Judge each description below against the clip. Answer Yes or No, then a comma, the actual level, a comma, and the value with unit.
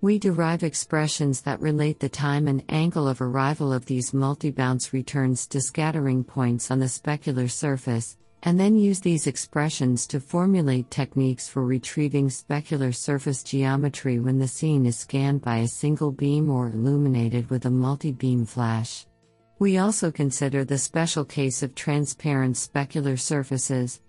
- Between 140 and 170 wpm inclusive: Yes, average, 150 wpm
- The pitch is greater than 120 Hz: Yes, low, 135 Hz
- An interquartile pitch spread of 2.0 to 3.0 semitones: Yes, average, 2.7 semitones